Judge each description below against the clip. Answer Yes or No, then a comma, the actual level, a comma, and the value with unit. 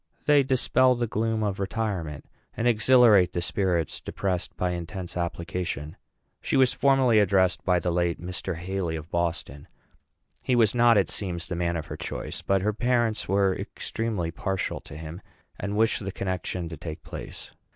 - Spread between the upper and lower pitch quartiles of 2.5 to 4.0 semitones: No, average, 4.4 semitones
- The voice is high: No, very low, 95 Hz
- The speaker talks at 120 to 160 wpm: No, average, 170 wpm